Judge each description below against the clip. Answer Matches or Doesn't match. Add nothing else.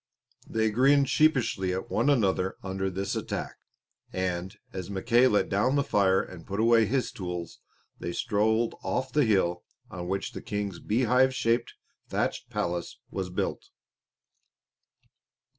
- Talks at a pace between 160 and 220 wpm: Doesn't match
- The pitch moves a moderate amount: Matches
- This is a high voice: Doesn't match